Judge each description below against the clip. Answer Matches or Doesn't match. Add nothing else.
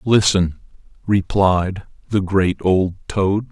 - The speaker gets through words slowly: Matches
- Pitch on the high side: Doesn't match